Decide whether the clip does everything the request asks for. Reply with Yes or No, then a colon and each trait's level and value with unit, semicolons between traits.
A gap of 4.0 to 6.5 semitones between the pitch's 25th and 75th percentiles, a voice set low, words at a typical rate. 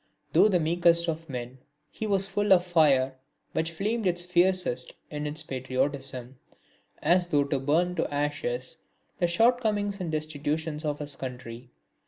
No: average, 4.6 semitones; medium, 155 Hz; average, 150 wpm